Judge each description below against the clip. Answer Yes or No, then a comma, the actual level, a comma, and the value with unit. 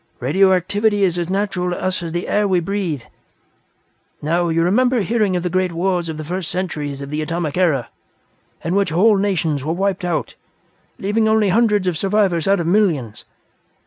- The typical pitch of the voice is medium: Yes, medium, 180 Hz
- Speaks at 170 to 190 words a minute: Yes, average, 180 wpm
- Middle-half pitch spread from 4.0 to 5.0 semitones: No, average, 3.3 semitones